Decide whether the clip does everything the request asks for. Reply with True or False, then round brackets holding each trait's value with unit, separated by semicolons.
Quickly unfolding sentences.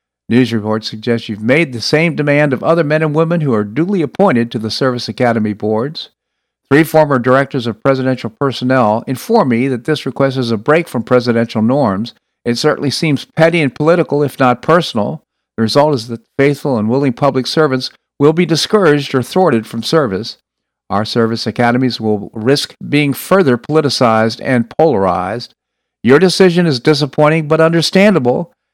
False (165 wpm)